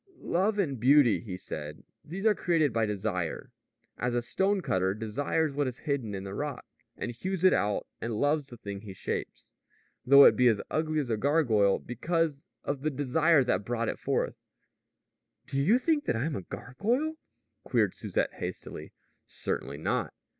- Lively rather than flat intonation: Yes, wide, 6.6 semitones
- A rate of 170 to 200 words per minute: Yes, average, 175 wpm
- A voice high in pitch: No, low, 135 Hz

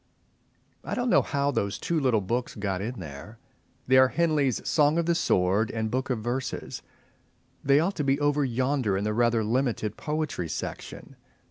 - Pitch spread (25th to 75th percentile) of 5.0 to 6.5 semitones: Yes, average, 5.3 semitones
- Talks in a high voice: No, low, 125 Hz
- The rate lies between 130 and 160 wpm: No, average, 185 wpm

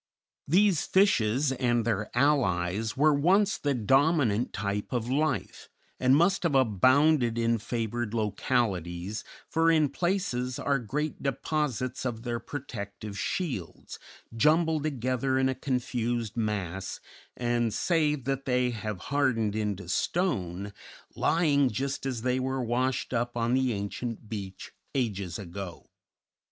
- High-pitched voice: No, low, 125 Hz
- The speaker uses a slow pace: Yes, slow, 125 wpm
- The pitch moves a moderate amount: Yes, average, 4.9 semitones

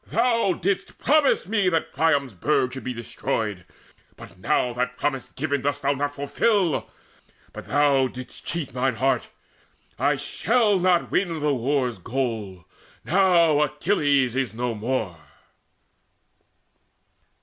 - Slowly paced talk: Yes, slow, 125 wpm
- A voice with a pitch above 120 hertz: Yes, medium, 140 Hz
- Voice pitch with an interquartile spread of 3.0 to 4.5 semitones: No, average, 5.1 semitones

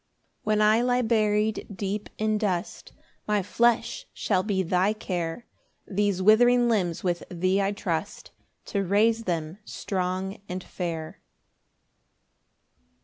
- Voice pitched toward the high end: Yes, high, 200 Hz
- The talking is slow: Yes, slow, 125 wpm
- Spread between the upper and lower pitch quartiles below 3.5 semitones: Yes, average, 2.9 semitones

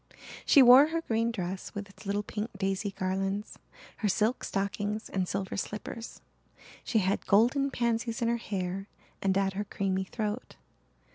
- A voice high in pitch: Yes, high, 205 Hz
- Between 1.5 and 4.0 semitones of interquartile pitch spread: Yes, average, 2.9 semitones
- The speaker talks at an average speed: Yes, average, 155 wpm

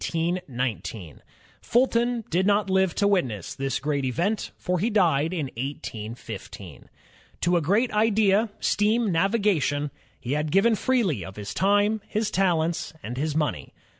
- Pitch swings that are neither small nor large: No, wide, 6.4 semitones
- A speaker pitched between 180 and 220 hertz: Yes, medium, 185 Hz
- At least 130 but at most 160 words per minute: Yes, average, 155 wpm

